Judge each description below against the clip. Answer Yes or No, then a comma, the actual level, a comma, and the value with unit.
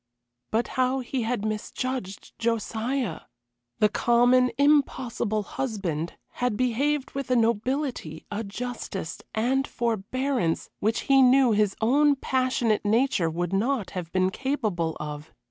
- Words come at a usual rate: No, slow, 125 wpm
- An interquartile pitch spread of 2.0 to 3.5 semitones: No, average, 4.3 semitones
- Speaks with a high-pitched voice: Yes, high, 235 Hz